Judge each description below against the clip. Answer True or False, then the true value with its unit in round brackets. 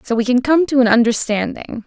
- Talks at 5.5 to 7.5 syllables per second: True (5.7 syllables/s)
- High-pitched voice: True (245 Hz)